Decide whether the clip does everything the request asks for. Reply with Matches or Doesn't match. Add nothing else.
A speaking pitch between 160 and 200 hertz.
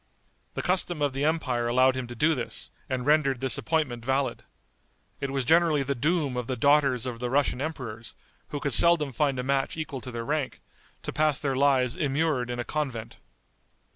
Doesn't match